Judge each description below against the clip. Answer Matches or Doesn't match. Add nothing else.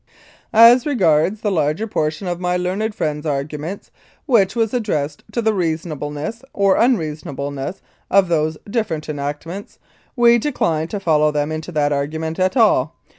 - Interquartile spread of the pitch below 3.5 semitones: Doesn't match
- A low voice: Doesn't match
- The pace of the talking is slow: Doesn't match